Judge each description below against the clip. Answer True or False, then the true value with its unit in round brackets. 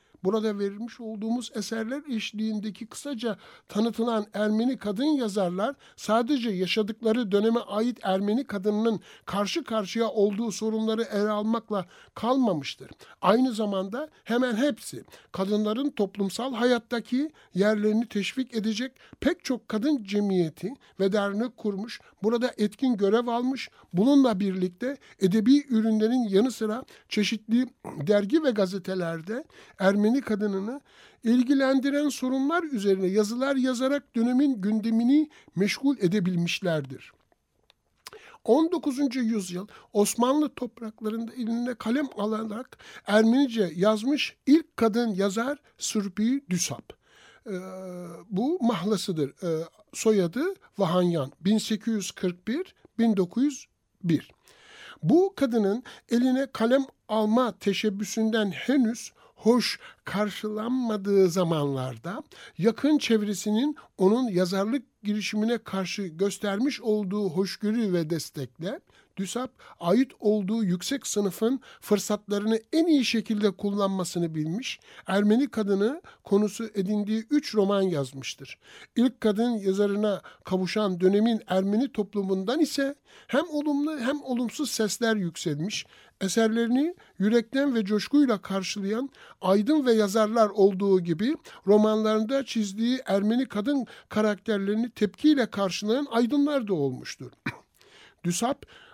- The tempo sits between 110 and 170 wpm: False (95 wpm)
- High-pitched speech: True (220 Hz)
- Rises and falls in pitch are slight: False (3.9 semitones)